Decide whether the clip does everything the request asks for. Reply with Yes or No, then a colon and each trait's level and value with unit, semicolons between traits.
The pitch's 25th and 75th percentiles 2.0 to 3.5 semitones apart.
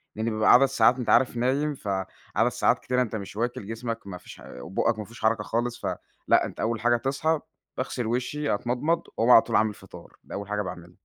Yes: average, 2.9 semitones